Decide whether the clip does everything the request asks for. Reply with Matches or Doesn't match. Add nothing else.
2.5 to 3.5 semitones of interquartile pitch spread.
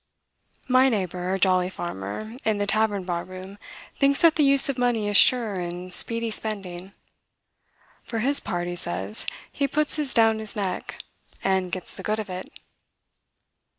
Doesn't match